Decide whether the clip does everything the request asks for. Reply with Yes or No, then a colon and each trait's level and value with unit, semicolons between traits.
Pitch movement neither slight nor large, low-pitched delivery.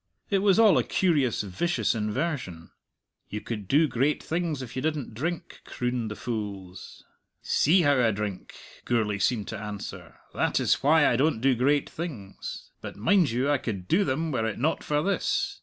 No: wide, 6.7 semitones; low, 130 Hz